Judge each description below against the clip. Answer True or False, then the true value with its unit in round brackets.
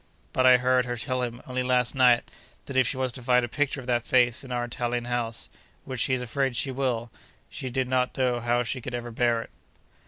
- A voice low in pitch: True (125 Hz)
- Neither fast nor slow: False (240 wpm)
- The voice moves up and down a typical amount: False (1.2 semitones)